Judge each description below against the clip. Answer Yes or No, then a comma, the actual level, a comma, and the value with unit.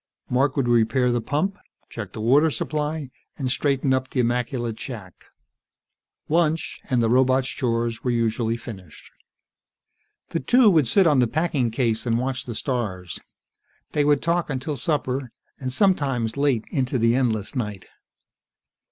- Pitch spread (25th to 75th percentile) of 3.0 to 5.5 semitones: Yes, average, 3.8 semitones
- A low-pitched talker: Yes, low, 130 Hz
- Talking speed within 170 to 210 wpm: No, average, 150 wpm